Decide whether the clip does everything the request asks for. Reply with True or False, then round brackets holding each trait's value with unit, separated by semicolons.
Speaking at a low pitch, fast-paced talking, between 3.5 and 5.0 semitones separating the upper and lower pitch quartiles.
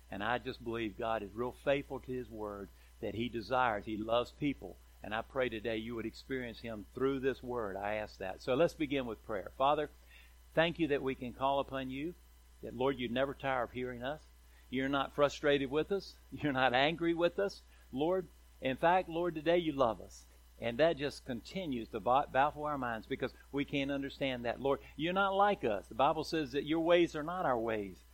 True (130 Hz; 210 wpm; 4.5 semitones)